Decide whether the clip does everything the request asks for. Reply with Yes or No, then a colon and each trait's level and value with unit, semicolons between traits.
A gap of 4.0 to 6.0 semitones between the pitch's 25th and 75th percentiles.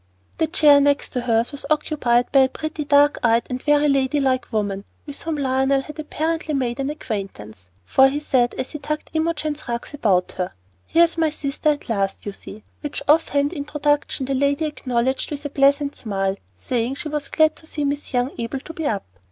No: average, 3.5 semitones